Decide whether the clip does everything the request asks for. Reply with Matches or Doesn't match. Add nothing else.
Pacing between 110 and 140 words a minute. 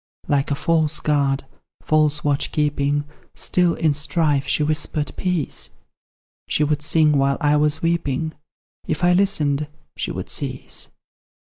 Matches